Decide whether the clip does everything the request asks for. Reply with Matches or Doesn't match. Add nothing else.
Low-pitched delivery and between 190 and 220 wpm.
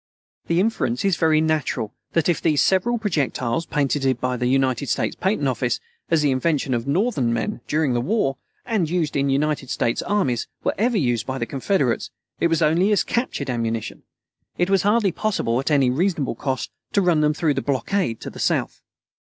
Doesn't match